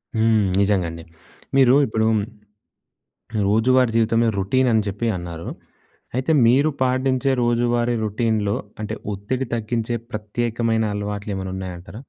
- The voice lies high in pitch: No, low, 110 Hz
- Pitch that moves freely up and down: No, average, 2.9 semitones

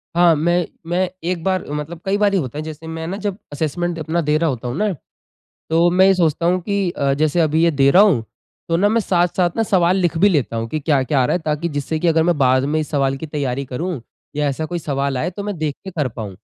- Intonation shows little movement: No, average, 3.6 semitones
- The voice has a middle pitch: Yes, medium, 160 Hz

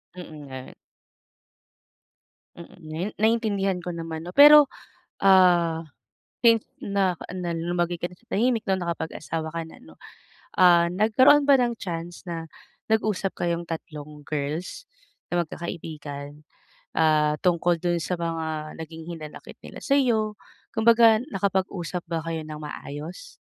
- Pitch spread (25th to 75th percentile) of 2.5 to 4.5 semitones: Yes, average, 3.8 semitones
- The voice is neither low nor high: Yes, medium, 175 Hz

